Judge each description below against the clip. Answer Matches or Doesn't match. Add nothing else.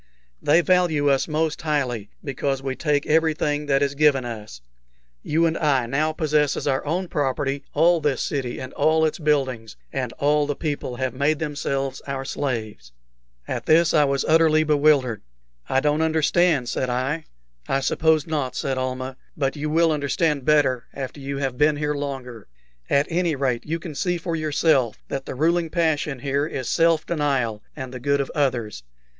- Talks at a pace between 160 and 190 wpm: Matches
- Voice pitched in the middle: Matches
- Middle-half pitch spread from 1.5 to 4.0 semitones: Matches